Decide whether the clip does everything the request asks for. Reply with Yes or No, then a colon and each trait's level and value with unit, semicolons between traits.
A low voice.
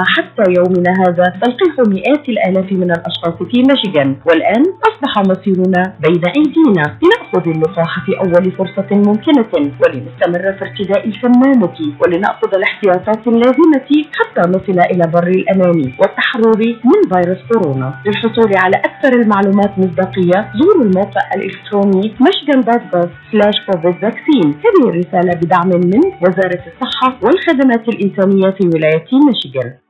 No: high, 195 Hz